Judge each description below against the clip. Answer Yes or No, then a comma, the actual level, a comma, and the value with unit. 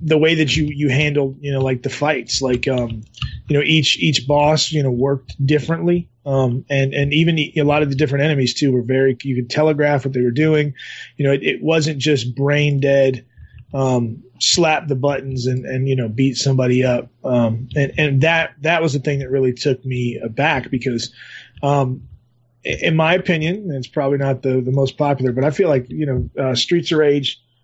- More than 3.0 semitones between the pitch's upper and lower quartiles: No, average, 2.7 semitones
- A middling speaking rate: No, fast, 215 wpm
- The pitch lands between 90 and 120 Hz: No, medium, 140 Hz